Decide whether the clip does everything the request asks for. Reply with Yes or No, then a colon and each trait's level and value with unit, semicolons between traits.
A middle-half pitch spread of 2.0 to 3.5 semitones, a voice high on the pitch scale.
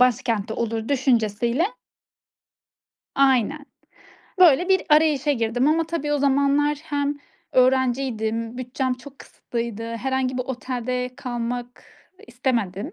Yes: average, 3.2 semitones; very high, 255 Hz